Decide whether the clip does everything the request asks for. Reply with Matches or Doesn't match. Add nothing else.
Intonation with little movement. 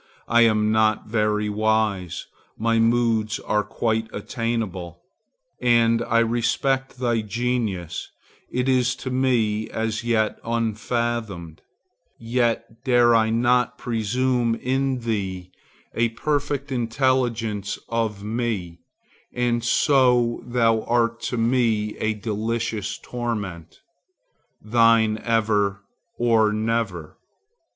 Matches